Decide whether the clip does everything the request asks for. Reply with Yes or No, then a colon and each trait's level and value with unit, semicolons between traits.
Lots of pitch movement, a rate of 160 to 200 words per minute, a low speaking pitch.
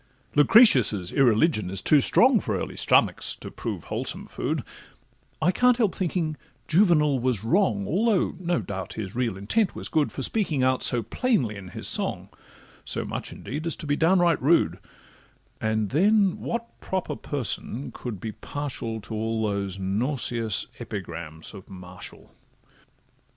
No: wide, 8.6 semitones; average, 150 wpm; low, 130 Hz